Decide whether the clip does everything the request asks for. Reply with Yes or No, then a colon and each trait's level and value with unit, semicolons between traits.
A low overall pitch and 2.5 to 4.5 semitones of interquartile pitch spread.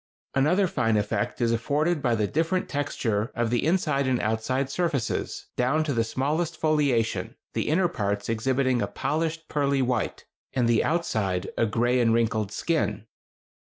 No: low, 130 Hz; average, 5.2 semitones